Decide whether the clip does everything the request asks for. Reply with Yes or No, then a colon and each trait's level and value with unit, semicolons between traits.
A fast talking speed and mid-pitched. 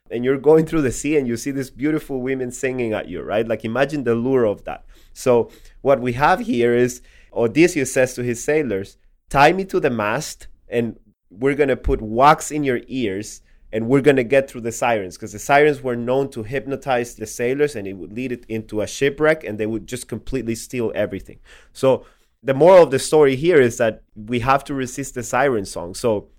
No: fast, 220 wpm; low, 125 Hz